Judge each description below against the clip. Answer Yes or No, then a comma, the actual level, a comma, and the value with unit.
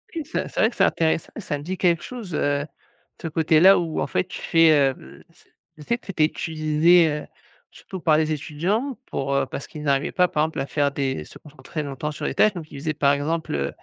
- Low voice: No, medium, 155 Hz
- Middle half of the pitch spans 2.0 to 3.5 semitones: Yes, average, 3.2 semitones